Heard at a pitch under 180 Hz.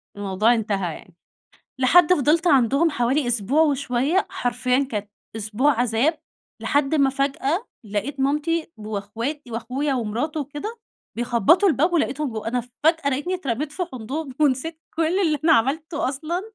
No: very high, 275 Hz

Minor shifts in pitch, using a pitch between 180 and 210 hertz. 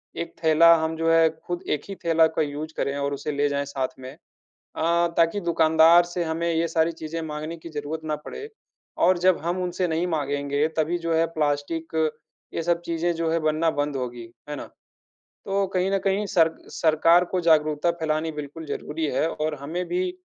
No: narrow, 2.0 semitones; medium, 160 Hz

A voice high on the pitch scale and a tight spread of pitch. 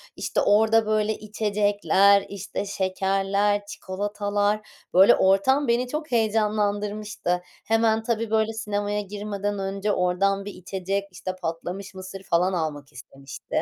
Yes: high, 205 Hz; narrow, 1.7 semitones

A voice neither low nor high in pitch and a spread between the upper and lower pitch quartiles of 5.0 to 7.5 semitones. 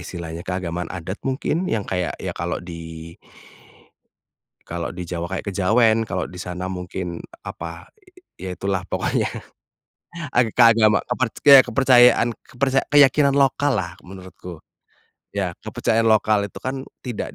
No: low, 100 Hz; wide, 5.6 semitones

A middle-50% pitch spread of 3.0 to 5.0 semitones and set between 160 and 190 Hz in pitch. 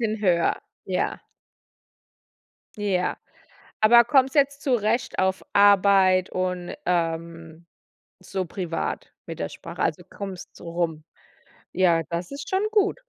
Yes: average, 4.4 semitones; medium, 185 Hz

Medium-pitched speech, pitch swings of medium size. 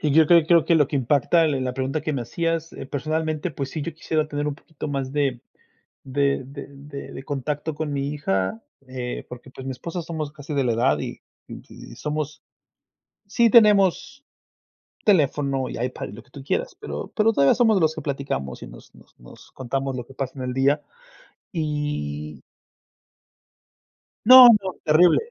Yes: medium, 145 Hz; average, 3.3 semitones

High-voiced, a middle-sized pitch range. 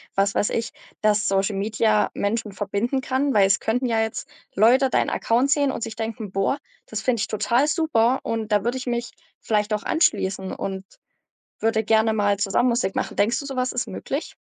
Yes: high, 225 Hz; average, 3.3 semitones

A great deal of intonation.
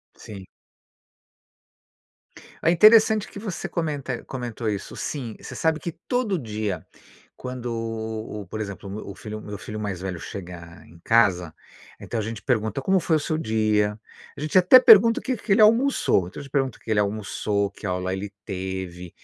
Yes: wide, 7.8 semitones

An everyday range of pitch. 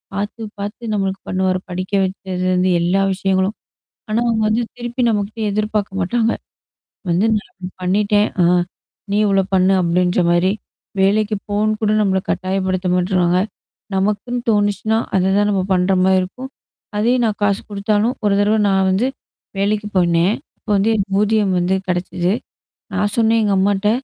No: narrow, 2.2 semitones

